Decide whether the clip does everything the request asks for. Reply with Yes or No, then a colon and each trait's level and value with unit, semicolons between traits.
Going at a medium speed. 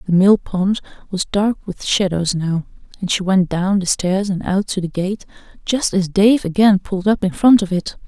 No: fast, 210 wpm